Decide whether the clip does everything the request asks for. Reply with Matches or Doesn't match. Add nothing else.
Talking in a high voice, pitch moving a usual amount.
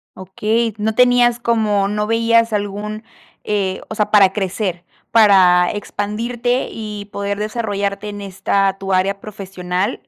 Doesn't match